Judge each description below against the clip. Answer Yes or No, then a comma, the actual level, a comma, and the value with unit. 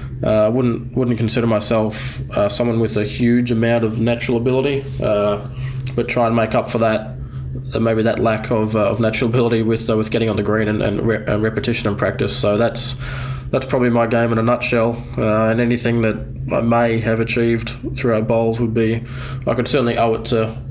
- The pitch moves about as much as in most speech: No, narrow, 2.1 semitones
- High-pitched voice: No, low, 115 Hz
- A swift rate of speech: Yes, fast, 210 wpm